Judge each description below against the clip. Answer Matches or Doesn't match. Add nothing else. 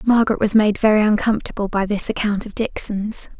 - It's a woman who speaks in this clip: Matches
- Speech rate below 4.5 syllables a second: Doesn't match